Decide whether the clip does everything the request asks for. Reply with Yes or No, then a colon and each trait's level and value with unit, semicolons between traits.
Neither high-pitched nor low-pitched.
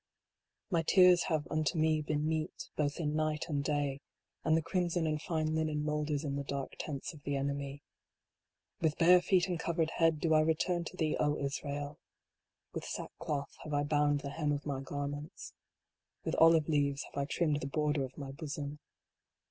Yes: medium, 150 Hz